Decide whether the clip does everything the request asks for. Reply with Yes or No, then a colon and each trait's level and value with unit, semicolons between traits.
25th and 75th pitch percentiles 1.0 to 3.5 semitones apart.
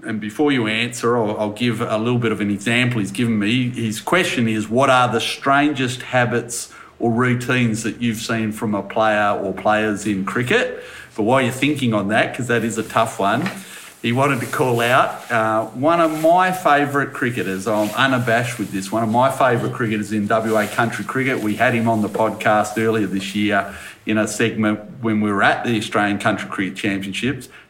Yes: average, 2.7 semitones